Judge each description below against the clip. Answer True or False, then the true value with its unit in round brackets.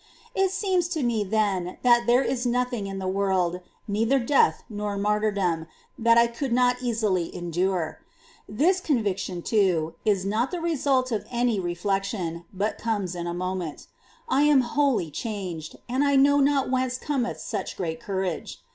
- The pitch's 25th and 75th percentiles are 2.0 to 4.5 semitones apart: False (5.4 semitones)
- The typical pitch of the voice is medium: False (215 Hz)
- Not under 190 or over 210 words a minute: False (165 wpm)